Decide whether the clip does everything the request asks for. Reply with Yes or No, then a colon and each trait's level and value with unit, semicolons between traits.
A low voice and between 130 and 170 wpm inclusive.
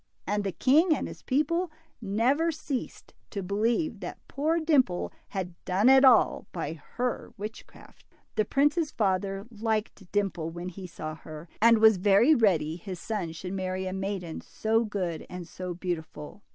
No: high, 200 Hz; average, 160 wpm